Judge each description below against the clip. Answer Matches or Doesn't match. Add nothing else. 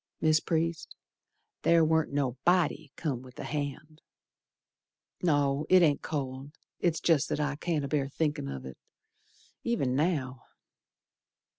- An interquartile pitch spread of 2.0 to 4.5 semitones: Matches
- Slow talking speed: Matches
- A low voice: Doesn't match